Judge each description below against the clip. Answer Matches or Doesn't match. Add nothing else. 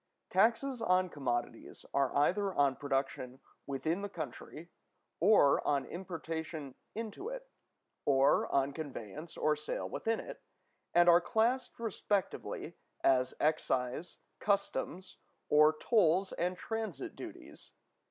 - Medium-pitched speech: Matches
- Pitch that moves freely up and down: Matches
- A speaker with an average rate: Doesn't match